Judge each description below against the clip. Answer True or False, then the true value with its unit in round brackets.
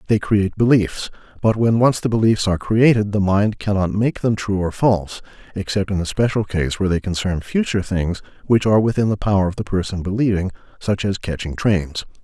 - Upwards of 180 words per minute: True (200 wpm)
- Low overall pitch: True (100 Hz)